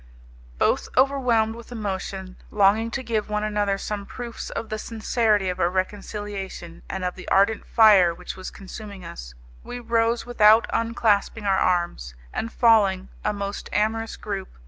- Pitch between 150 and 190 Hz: No, high, 210 Hz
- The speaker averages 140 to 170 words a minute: Yes, average, 155 wpm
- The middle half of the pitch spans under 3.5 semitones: Yes, average, 2.8 semitones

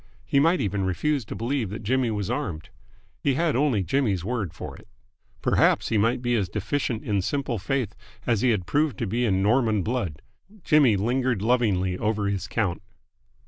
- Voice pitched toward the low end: Yes, low, 110 Hz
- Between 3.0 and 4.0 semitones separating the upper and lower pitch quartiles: No, average, 4.6 semitones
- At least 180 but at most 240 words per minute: Yes, average, 185 wpm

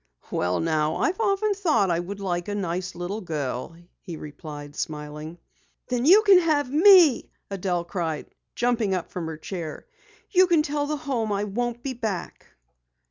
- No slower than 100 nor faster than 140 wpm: No, average, 165 wpm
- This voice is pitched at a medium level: No, high, 200 Hz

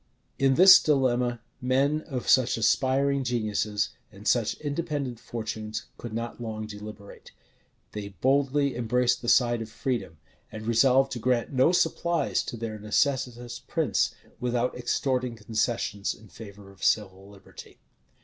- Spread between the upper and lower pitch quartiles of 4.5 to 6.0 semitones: No, average, 3.4 semitones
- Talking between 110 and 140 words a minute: Yes, slow, 135 wpm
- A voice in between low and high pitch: No, low, 120 Hz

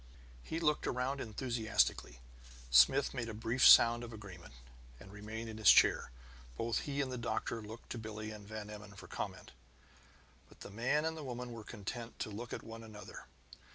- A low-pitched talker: Yes, low, 115 Hz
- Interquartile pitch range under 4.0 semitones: Yes, average, 2.7 semitones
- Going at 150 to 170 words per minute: No, average, 185 wpm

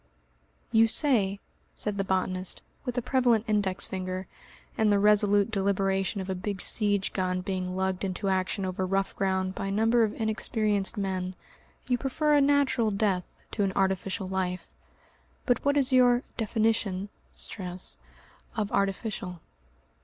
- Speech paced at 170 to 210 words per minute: No, average, 145 wpm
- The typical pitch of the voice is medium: No, high, 200 Hz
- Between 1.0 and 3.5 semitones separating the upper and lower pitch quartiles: Yes, average, 2.9 semitones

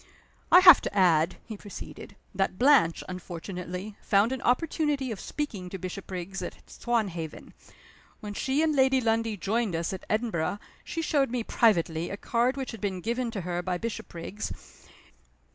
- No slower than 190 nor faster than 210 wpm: No, average, 160 wpm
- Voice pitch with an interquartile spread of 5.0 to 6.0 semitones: Yes, wide, 5.4 semitones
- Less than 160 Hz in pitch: No, high, 210 Hz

